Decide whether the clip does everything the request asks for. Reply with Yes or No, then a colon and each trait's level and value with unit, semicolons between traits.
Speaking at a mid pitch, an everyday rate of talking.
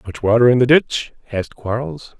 No: low, 115 Hz; average, 190 wpm